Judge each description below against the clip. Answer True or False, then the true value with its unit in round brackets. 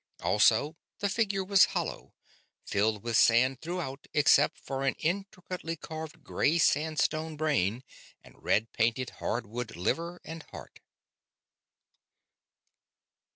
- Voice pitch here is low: False (150 Hz)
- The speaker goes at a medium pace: False (110 wpm)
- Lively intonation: True (6.0 semitones)